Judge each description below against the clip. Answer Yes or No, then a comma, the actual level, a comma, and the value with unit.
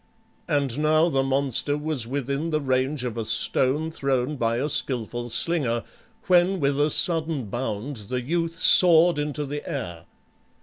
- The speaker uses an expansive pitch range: No, average, 3.8 semitones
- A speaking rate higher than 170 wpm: No, average, 155 wpm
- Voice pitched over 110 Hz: Yes, medium, 140 Hz